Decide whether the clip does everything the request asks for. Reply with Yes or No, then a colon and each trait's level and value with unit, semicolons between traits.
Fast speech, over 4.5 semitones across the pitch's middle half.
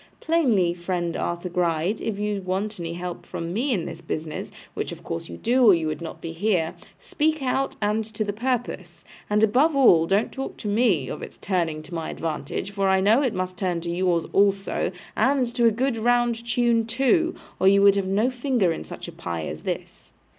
Yes: fast, 210 wpm; wide, 5.6 semitones